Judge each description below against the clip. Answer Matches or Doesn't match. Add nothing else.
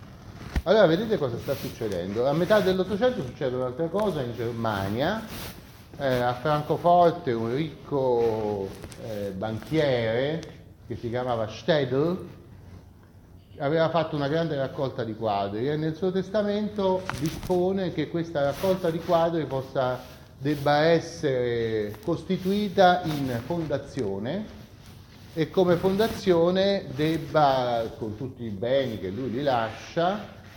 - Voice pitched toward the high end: Doesn't match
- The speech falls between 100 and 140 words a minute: Matches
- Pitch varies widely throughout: Matches